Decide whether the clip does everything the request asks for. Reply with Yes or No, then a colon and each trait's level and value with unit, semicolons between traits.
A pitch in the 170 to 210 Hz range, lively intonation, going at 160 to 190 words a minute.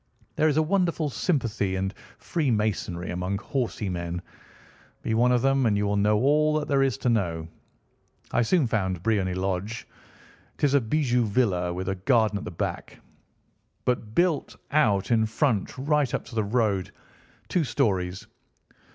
No: low, 110 Hz; wide, 6.0 semitones; average, 165 wpm